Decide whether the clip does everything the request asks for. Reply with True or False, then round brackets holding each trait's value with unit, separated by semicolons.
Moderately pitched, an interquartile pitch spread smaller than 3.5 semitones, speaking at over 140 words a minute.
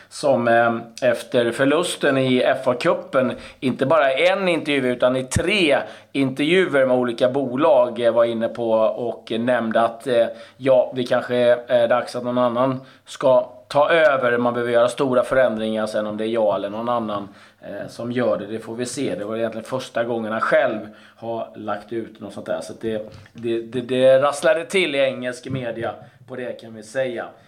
False (120 Hz; 2.7 semitones; 185 wpm)